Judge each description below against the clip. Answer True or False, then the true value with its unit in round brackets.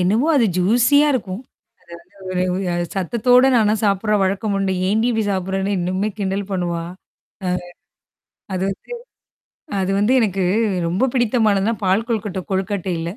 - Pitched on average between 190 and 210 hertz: True (200 Hz)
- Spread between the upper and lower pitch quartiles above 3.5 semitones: False (3.0 semitones)